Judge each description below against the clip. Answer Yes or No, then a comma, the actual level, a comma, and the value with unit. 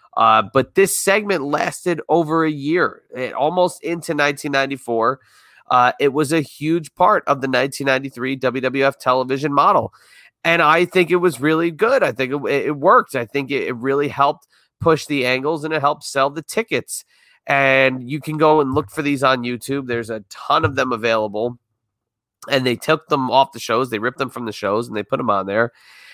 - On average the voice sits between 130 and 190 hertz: Yes, medium, 140 Hz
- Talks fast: No, average, 195 wpm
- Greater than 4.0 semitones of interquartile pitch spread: No, average, 3.7 semitones